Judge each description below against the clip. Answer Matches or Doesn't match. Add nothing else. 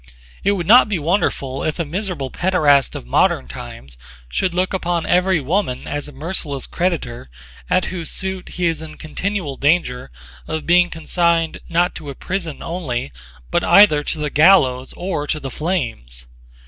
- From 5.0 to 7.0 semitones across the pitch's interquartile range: Doesn't match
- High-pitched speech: Doesn't match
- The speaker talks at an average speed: Matches